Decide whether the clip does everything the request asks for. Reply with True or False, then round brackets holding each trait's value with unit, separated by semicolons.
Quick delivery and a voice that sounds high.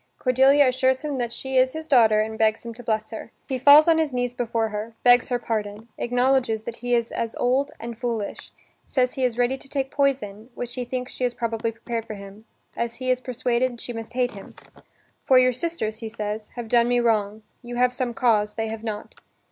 True (220 wpm; 240 Hz)